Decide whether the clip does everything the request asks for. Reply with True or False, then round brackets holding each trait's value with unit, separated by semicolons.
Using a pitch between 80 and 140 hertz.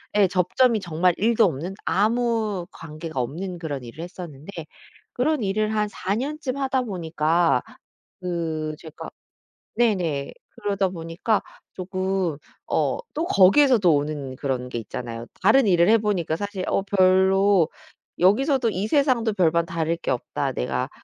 False (185 Hz)